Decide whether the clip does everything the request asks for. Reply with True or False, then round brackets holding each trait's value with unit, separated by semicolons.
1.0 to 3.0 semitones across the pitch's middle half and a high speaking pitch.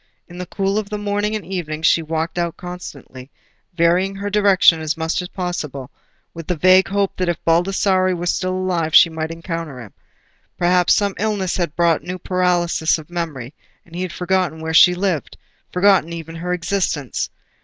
False (2.4 semitones; 175 Hz)